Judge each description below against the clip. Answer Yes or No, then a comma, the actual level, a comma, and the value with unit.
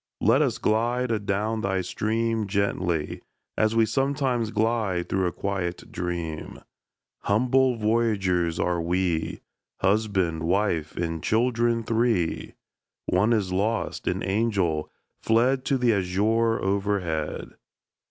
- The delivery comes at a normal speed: No, slow, 115 wpm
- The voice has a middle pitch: No, low, 105 Hz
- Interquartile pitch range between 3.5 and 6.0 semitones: Yes, average, 4.2 semitones